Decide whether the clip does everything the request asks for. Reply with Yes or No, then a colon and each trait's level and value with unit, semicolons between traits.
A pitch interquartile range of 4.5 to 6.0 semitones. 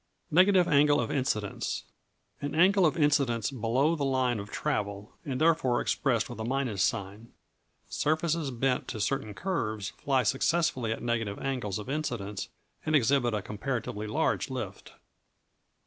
Yes: average, 5.3 semitones